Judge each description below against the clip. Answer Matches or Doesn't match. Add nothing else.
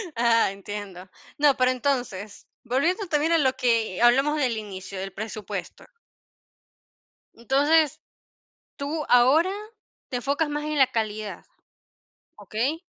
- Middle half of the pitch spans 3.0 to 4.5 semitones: Doesn't match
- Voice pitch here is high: Matches